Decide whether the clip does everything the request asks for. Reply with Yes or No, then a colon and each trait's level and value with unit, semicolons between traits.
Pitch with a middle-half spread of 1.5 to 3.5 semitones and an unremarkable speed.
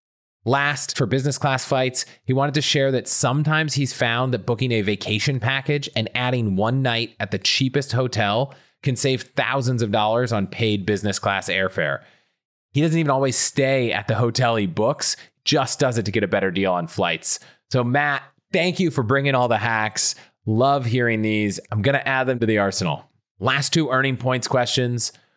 No: average, 3.9 semitones; average, 190 wpm